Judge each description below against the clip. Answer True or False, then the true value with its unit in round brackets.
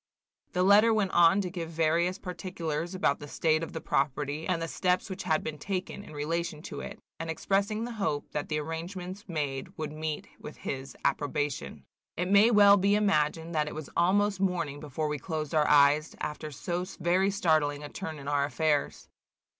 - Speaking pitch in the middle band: True (165 Hz)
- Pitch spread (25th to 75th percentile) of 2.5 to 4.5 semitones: True (3.8 semitones)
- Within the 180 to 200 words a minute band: True (190 wpm)